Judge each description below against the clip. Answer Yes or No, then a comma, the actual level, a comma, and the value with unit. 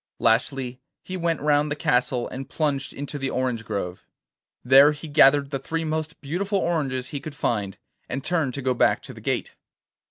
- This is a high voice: No, medium, 140 Hz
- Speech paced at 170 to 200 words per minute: Yes, average, 185 wpm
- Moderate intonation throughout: Yes, average, 3.3 semitones